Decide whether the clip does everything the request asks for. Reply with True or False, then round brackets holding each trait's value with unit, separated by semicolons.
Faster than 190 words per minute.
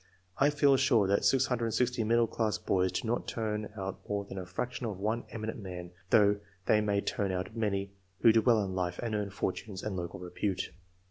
True (200 wpm)